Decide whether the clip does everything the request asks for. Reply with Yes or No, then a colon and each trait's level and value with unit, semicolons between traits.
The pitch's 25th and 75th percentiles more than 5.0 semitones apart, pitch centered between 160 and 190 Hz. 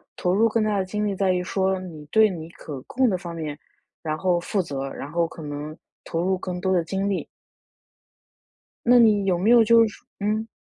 No: average, 4.0 semitones; medium, 185 Hz